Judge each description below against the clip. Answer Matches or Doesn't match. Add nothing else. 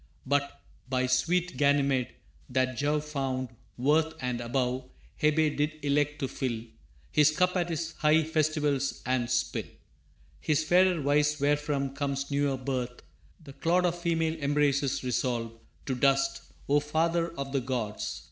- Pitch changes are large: Doesn't match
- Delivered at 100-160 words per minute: Matches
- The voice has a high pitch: Doesn't match